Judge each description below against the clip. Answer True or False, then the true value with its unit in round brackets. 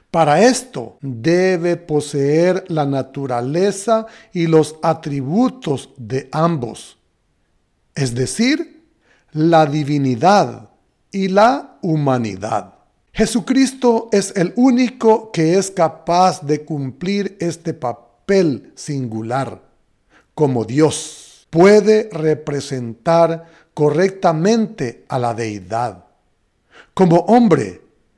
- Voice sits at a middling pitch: True (160 Hz)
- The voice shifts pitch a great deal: True (6.3 semitones)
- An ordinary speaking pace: False (85 wpm)